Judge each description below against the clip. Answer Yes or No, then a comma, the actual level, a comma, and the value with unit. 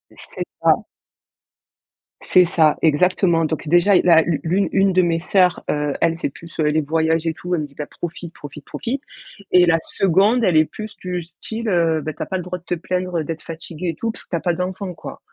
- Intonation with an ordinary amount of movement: No, narrow, 2.3 semitones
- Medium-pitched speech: Yes, medium, 170 Hz